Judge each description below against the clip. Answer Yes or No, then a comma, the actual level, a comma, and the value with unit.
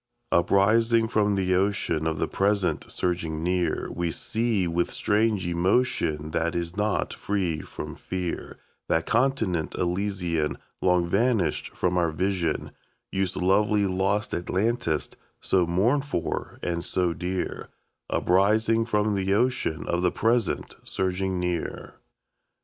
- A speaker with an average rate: No, slow, 125 wpm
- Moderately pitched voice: No, very low, 95 Hz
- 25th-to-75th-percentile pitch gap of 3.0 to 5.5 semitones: Yes, average, 3.4 semitones